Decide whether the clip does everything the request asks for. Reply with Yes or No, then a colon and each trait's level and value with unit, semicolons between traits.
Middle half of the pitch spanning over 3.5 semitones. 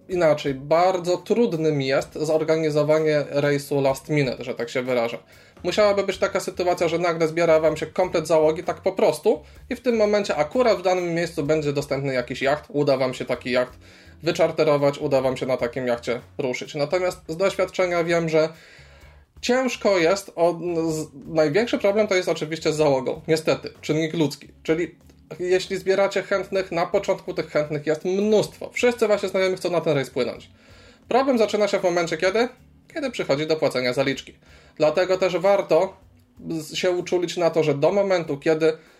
Yes: average, 4.3 semitones